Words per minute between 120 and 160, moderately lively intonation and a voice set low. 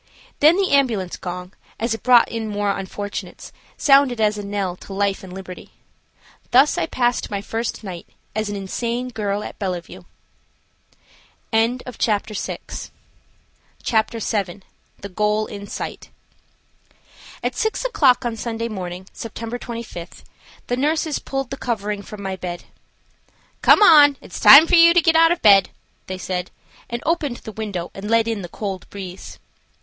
No: average, 150 wpm; average, 3.9 semitones; high, 215 Hz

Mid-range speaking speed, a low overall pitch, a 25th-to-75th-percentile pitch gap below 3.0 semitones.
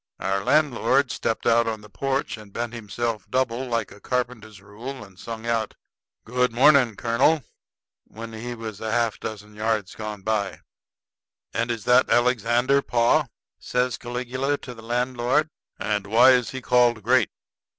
Yes: average, 150 wpm; low, 115 Hz; narrow, 2.5 semitones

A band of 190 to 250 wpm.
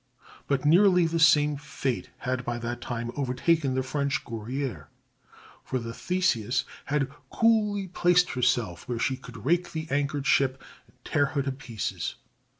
No: average, 150 wpm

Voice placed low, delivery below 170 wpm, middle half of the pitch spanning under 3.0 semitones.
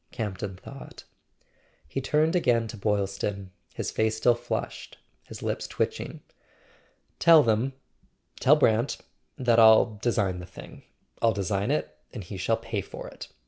No: low, 110 Hz; average, 140 wpm; average, 3.6 semitones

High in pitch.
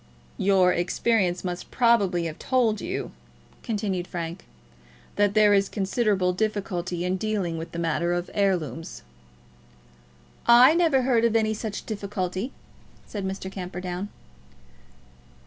Yes: high, 195 Hz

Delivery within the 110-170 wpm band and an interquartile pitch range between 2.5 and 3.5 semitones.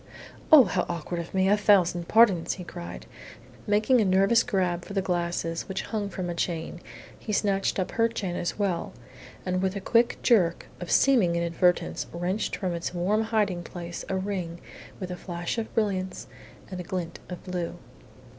No: average, 180 wpm; average, 2.9 semitones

